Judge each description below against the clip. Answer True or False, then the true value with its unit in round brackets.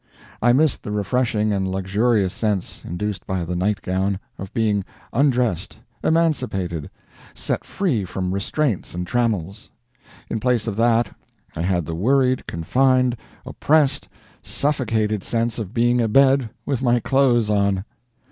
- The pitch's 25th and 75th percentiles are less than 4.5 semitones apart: False (4.8 semitones)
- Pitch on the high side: False (110 Hz)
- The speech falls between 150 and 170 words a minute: False (135 wpm)